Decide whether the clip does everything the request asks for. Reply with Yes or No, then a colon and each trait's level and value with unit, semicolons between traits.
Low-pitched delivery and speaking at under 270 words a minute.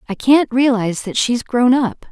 No: high, 240 Hz; average, 200 wpm